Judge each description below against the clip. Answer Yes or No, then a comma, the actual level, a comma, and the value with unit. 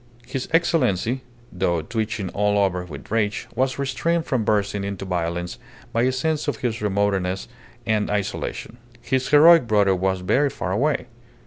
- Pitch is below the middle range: Yes, low, 105 Hz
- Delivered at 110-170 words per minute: Yes, average, 150 wpm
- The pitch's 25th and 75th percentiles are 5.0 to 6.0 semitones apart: Yes, average, 5.3 semitones